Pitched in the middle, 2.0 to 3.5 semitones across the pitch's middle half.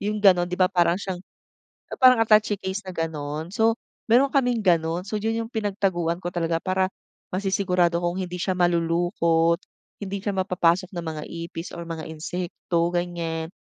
Yes: medium, 180 Hz; average, 2.9 semitones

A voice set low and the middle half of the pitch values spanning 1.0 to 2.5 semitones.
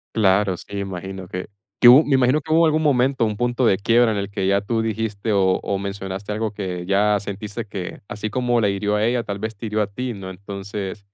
No: low, 105 Hz; average, 2.9 semitones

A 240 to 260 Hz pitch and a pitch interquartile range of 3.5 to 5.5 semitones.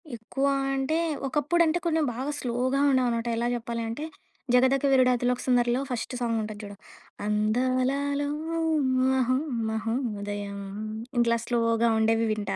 No: high, 245 Hz; narrow, 2.6 semitones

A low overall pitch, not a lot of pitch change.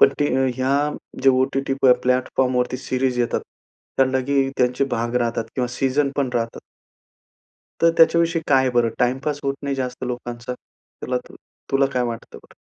Yes: low, 130 Hz; narrow, 1.6 semitones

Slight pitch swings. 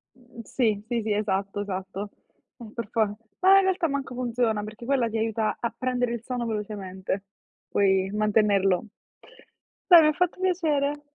No: average, 4.0 semitones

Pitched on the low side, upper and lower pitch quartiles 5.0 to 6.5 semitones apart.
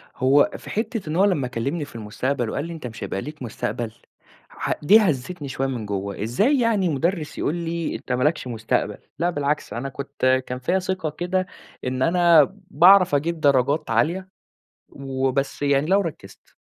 No: medium, 145 Hz; average, 5.3 semitones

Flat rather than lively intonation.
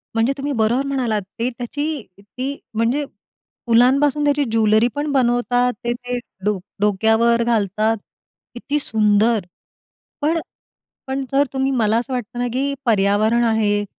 No: average, 3.6 semitones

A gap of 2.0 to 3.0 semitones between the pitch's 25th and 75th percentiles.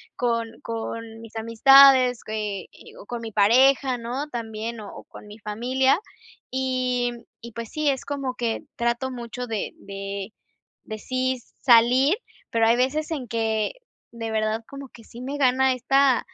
Yes: average, 2.7 semitones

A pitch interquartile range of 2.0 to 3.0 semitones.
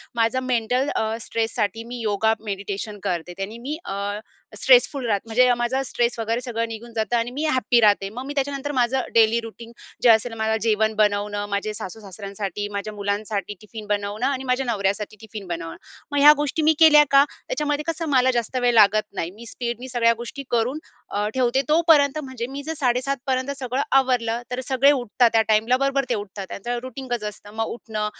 No: average, 3.6 semitones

